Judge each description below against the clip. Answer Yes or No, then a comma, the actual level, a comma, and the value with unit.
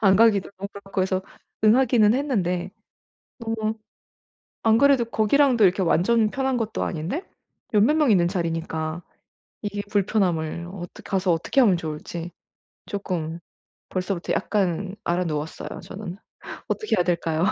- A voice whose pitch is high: Yes, high, 195 Hz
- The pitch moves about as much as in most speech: Yes, average, 4.4 semitones